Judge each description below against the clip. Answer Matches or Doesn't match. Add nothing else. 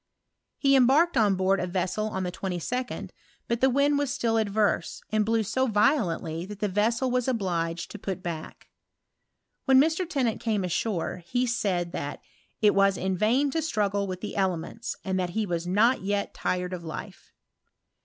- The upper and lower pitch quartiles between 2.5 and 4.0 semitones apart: Doesn't match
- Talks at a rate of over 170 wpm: Matches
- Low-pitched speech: Doesn't match